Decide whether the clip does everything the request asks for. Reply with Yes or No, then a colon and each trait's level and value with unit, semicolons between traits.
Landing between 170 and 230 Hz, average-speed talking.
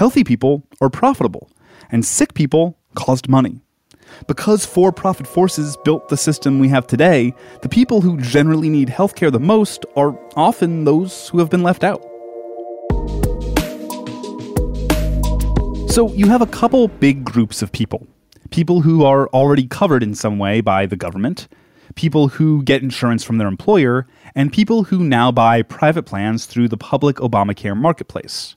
No: medium, 140 Hz; average, 155 wpm